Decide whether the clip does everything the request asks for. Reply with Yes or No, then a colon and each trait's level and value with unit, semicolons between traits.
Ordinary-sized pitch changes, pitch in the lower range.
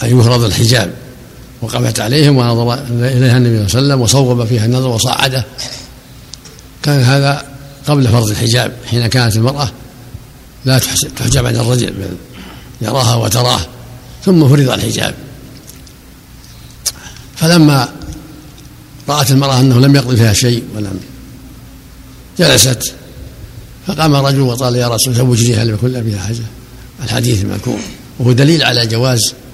No: narrow, 2.2 semitones; low, 125 Hz